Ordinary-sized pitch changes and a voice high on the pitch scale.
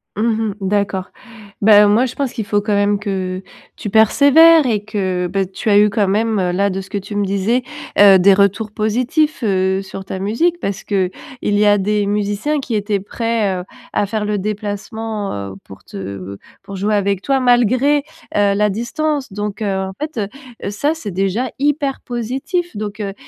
Yes: average, 3.1 semitones; high, 210 Hz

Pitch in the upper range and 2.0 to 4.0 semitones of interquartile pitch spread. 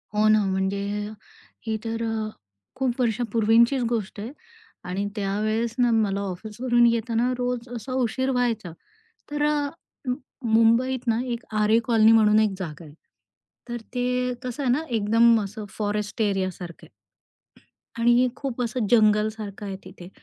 Yes: high, 225 Hz; narrow, 2.6 semitones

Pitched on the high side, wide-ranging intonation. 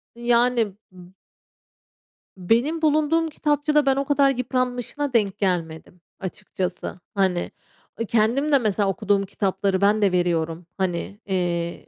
Yes: high, 205 Hz; wide, 6.3 semitones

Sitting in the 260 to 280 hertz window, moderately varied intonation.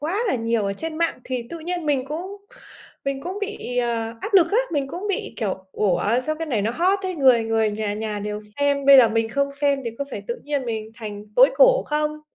No: very high, 275 Hz; wide, 6.3 semitones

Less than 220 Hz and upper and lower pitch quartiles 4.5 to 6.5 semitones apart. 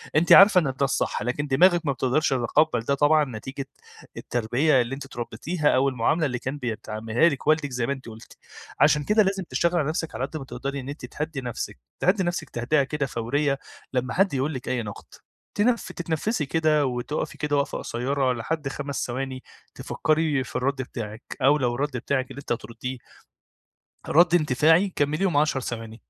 No: medium, 140 Hz; average, 3.7 semitones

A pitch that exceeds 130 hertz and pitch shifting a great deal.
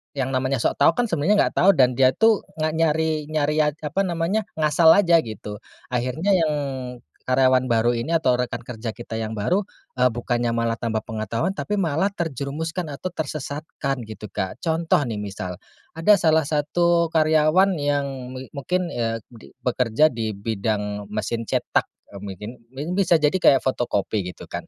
Yes: medium, 140 Hz; wide, 5.7 semitones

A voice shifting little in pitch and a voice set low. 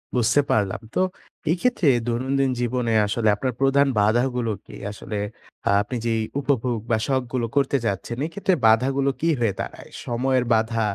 No: average, 3.2 semitones; low, 125 Hz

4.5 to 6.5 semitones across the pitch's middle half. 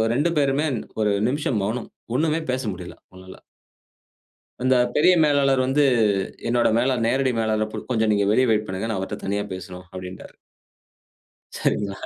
Yes: average, 5.0 semitones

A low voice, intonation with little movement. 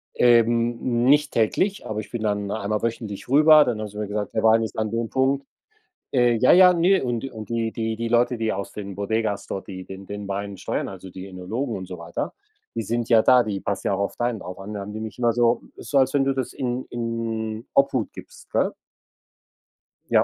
No: low, 115 Hz; average, 3.0 semitones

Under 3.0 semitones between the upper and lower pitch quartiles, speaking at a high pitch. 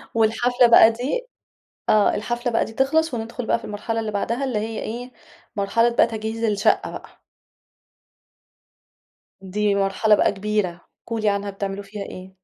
Yes: narrow, 2.6 semitones; high, 220 Hz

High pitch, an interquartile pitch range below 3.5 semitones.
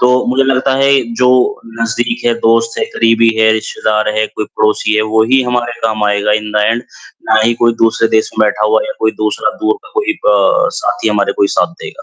No: low, 115 Hz; narrow, 2.4 semitones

